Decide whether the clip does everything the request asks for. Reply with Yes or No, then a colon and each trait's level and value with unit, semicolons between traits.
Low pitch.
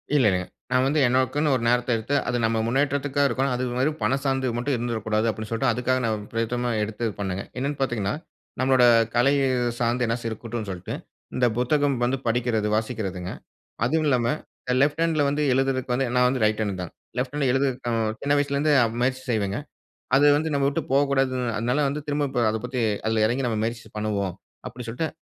Yes: low, 125 Hz